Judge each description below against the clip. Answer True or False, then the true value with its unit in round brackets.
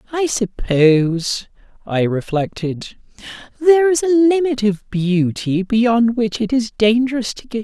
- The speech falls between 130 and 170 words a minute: True (135 wpm)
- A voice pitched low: False (225 Hz)